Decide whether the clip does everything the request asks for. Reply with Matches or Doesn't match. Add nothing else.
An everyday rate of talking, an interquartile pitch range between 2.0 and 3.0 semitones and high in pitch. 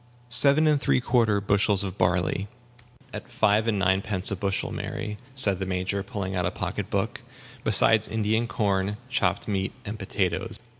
Doesn't match